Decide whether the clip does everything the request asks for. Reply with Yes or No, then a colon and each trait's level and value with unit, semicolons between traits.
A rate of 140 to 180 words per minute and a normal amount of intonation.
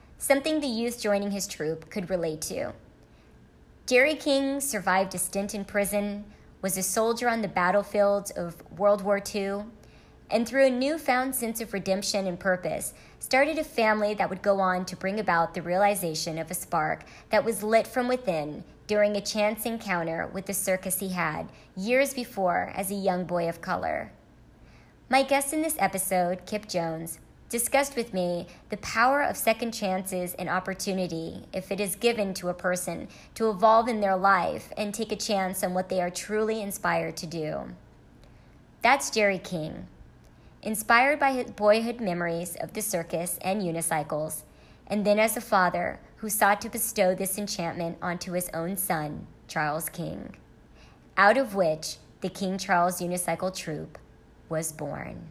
Yes: average, 165 wpm; average, 3.6 semitones